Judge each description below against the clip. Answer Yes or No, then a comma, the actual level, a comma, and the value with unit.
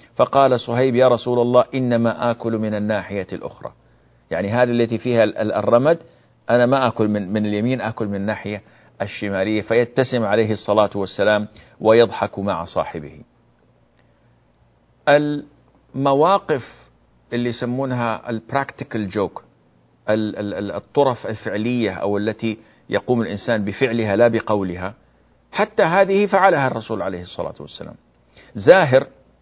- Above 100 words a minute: Yes, average, 110 wpm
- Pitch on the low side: Yes, low, 115 Hz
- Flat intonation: No, average, 3.2 semitones